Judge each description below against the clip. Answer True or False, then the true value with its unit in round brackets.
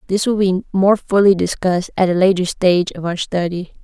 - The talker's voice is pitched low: False (185 Hz)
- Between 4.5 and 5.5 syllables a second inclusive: False (6.0 syllables/s)